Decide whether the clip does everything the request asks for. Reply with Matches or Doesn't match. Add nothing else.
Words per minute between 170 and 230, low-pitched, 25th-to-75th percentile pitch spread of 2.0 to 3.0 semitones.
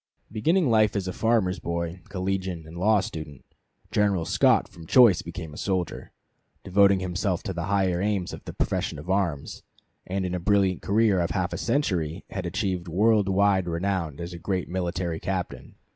Matches